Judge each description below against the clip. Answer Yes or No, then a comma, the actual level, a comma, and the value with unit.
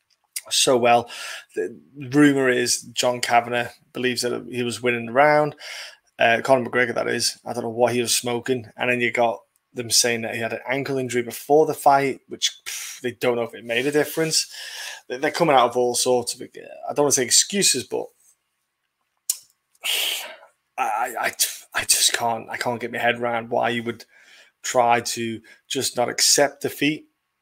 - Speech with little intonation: No, average, 3.2 semitones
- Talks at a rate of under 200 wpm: Yes, average, 180 wpm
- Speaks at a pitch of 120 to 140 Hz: Yes, low, 125 Hz